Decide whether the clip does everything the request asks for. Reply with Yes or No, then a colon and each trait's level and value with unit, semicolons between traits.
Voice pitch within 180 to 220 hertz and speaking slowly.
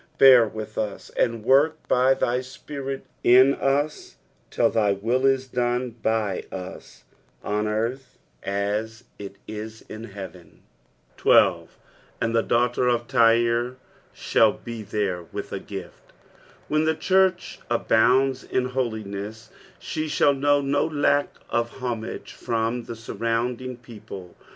No: low, 120 Hz; slow, 120 wpm